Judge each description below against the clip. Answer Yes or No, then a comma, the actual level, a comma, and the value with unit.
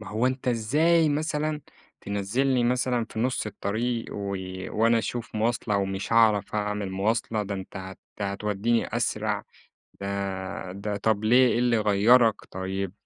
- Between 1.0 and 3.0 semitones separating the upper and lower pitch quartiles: No, average, 3.5 semitones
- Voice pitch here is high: No, low, 110 Hz